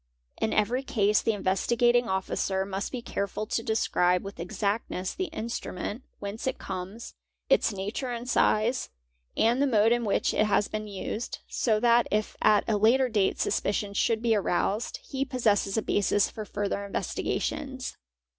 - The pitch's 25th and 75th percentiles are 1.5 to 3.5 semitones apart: Yes, average, 2.9 semitones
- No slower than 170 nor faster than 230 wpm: No, average, 160 wpm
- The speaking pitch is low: No, high, 215 Hz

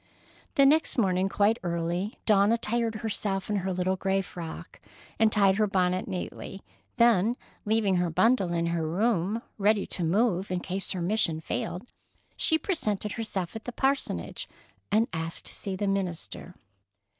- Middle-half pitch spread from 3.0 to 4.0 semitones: Yes, average, 3.6 semitones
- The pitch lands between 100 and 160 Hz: No, high, 195 Hz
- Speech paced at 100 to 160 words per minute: Yes, average, 155 wpm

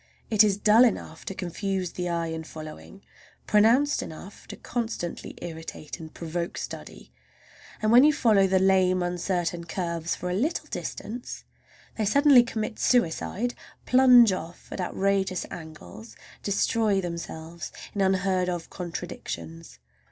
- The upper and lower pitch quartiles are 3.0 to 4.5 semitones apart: Yes, average, 4.2 semitones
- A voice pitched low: No, high, 190 Hz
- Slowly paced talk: Yes, slow, 130 wpm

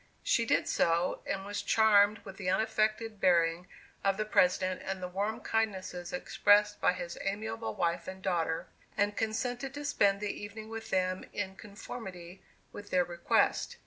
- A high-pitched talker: Yes, high, 200 Hz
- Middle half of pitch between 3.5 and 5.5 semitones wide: No, average, 2.9 semitones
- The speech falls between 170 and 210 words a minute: No, average, 160 wpm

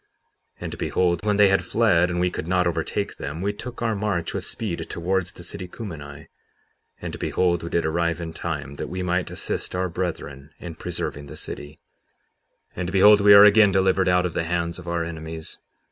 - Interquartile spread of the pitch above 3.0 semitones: No, narrow, 2.5 semitones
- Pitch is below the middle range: Yes, very low, 90 Hz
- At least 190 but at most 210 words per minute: Yes, fast, 205 wpm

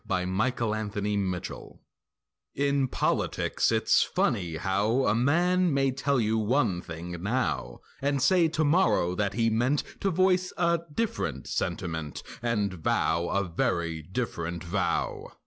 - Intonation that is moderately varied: No, wide, 7.7 semitones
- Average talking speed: No, slow, 130 wpm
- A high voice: No, low, 110 Hz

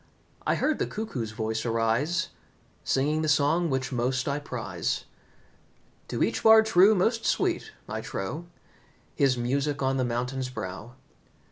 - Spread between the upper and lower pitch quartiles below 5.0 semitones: No, wide, 5.5 semitones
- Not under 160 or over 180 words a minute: No, average, 140 wpm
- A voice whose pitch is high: No, low, 135 Hz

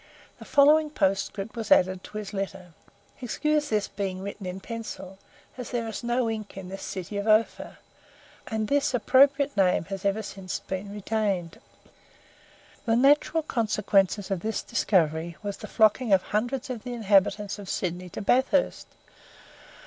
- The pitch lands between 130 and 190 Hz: No, high, 210 Hz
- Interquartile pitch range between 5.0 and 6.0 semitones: No, average, 3.8 semitones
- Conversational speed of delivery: Yes, average, 155 wpm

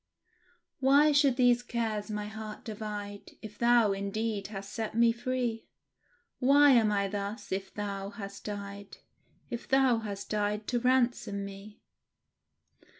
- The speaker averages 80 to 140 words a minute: Yes, slow, 135 wpm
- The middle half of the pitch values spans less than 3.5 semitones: Yes, average, 3.0 semitones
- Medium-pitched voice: No, high, 215 Hz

